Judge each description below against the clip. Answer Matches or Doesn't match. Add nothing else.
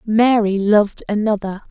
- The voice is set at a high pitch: Matches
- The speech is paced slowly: Matches